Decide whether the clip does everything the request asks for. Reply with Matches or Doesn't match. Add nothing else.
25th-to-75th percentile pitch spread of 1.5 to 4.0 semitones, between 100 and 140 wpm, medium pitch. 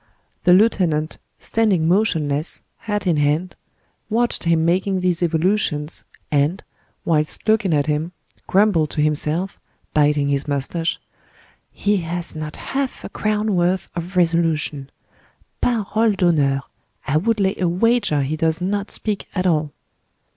Doesn't match